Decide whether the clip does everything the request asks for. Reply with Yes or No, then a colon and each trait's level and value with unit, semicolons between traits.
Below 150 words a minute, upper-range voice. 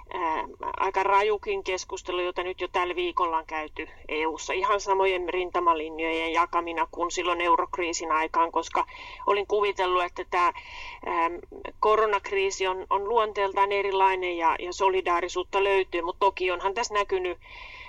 Yes: average, 130 wpm; high, 195 Hz